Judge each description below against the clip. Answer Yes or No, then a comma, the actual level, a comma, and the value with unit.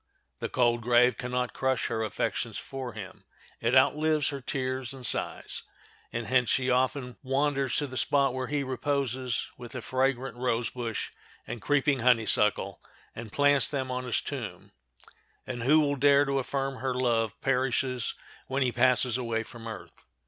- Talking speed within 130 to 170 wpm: Yes, average, 165 wpm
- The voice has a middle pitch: No, low, 130 Hz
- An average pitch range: No, narrow, 2.2 semitones